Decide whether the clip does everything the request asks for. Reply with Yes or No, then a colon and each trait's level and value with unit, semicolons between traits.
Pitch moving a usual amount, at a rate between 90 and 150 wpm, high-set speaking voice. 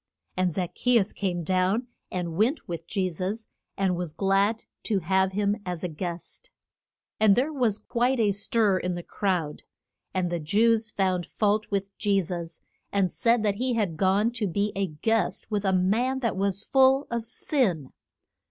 No: average, 3.6 semitones; average, 180 wpm; high, 195 Hz